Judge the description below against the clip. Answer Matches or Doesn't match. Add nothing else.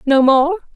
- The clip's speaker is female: Matches